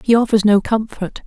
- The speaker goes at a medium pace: Yes, average, 190 wpm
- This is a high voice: Yes, high, 215 Hz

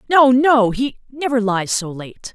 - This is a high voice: Yes, high, 240 Hz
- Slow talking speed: Yes, slow, 130 wpm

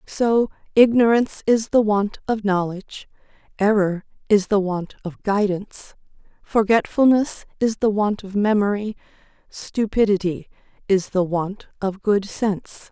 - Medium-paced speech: No, slow, 120 wpm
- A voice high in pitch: Yes, high, 205 Hz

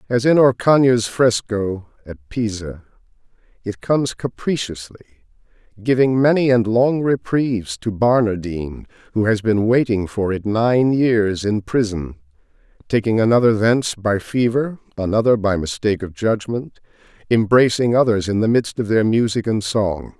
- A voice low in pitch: Yes, low, 110 Hz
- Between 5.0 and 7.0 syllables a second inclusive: No, 4.6 syllables/s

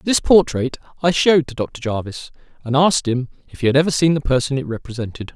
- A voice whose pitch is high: No, medium, 140 Hz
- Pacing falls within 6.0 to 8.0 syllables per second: Yes, 6.2 syllables/s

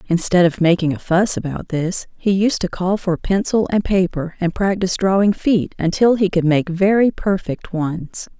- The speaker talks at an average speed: Yes, average, 185 wpm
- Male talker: No, female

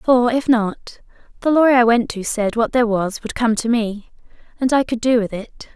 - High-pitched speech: Yes, high, 235 Hz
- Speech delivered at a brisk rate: Yes, fast, 220 wpm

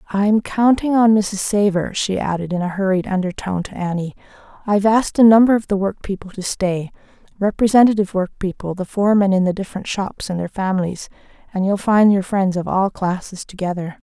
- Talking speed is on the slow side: No, average, 170 wpm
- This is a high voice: Yes, high, 195 Hz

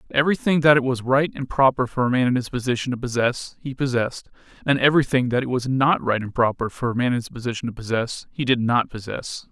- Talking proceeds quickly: Yes, fast, 240 wpm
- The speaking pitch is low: Yes, low, 125 Hz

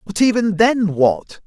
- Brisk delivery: No, average, 165 wpm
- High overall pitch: Yes, high, 200 Hz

